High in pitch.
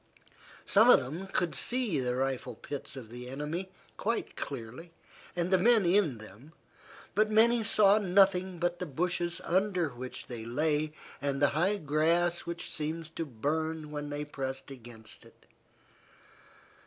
No: medium, 160 Hz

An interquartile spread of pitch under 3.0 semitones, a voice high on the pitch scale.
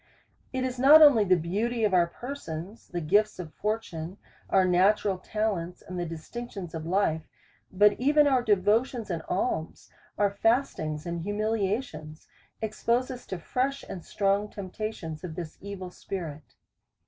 No: average, 4.7 semitones; high, 200 Hz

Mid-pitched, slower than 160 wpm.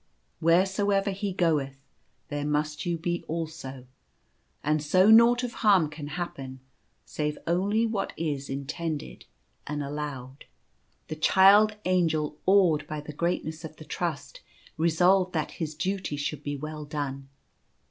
Yes: medium, 160 Hz; average, 140 wpm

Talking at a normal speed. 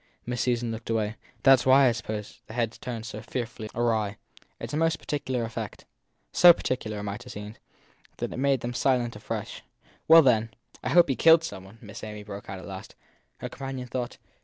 No: fast, 210 wpm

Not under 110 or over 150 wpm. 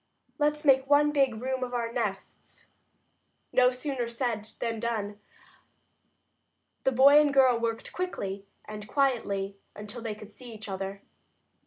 Yes: average, 140 wpm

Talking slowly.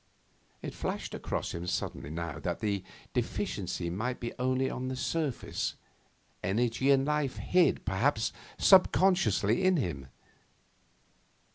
Yes: slow, 120 wpm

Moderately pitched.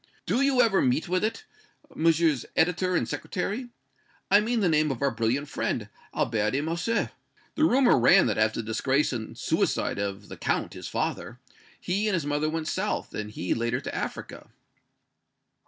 Yes: medium, 155 Hz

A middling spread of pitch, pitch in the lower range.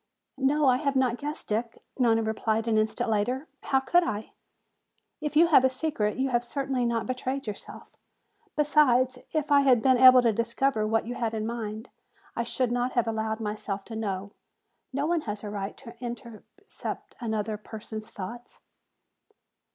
No: average, 3.4 semitones; high, 240 Hz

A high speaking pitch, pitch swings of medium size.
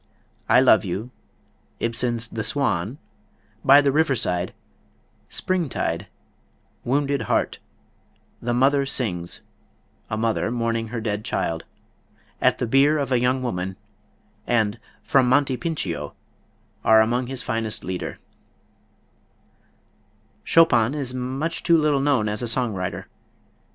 No: low, 120 Hz; average, 4.1 semitones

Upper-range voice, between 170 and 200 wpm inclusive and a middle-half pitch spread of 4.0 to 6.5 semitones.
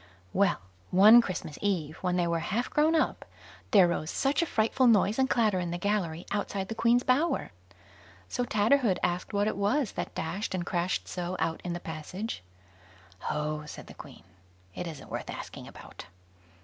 Yes: high, 195 Hz; average, 175 wpm; average, 4.9 semitones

